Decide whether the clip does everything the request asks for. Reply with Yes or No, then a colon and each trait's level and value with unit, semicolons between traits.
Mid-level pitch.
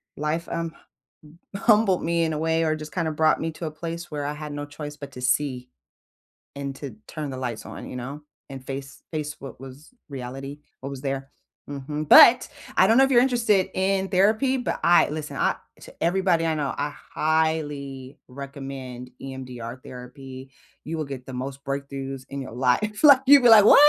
Yes: medium, 150 Hz